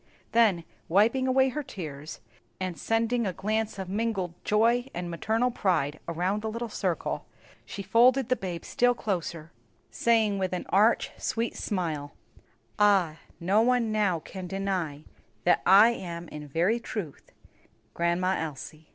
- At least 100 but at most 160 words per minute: Yes, average, 145 wpm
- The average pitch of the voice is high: Yes, high, 195 Hz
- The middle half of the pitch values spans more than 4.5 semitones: Yes, average, 4.9 semitones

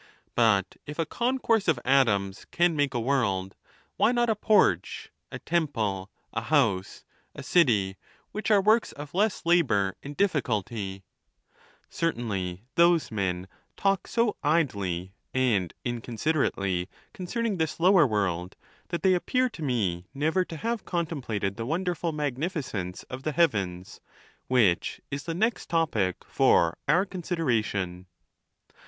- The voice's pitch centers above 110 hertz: Yes, medium, 140 Hz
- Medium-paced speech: No, slow, 130 wpm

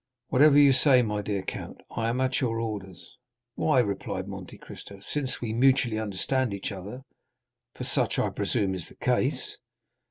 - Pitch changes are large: No, average, 4.5 semitones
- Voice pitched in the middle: No, low, 115 Hz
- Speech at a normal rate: Yes, average, 160 wpm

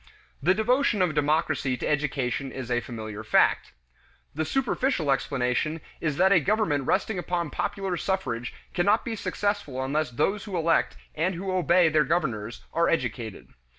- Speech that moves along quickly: No, average, 150 wpm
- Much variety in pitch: Yes, wide, 6.2 semitones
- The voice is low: No, medium, 155 Hz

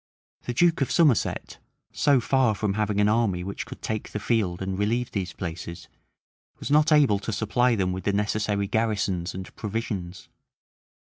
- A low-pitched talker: Yes, low, 105 Hz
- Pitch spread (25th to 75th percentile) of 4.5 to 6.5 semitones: No, average, 3.6 semitones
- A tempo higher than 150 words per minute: Yes, average, 170 wpm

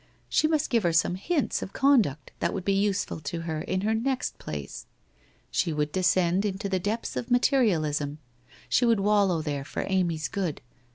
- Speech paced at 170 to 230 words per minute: Yes, average, 180 wpm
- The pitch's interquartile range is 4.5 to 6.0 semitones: Yes, average, 5.3 semitones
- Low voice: No, high, 190 Hz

